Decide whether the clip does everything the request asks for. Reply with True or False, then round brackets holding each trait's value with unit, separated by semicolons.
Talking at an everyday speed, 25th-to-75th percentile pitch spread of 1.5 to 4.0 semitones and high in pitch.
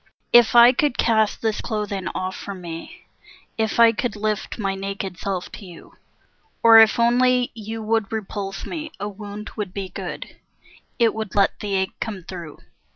True (170 wpm; 2.7 semitones; 210 Hz)